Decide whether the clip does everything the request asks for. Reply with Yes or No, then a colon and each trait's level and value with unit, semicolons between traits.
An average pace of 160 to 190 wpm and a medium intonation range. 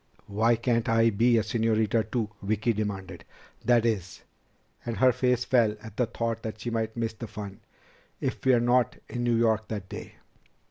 No: average, 180 wpm; narrow, 1.7 semitones